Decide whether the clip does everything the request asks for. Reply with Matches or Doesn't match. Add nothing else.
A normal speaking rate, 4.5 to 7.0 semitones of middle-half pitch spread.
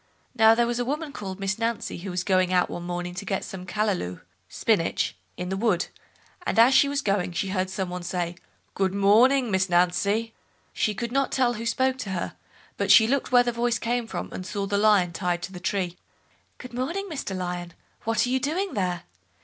Doesn't match